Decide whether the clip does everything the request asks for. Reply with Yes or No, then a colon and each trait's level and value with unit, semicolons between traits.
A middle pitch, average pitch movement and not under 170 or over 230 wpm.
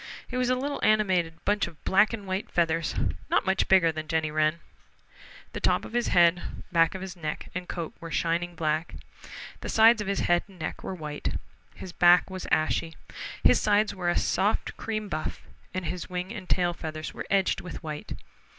Yes: medium, 180 Hz; average, 3.2 semitones; average, 195 wpm